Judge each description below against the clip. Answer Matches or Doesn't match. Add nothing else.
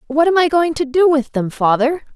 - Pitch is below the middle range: Doesn't match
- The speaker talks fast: Matches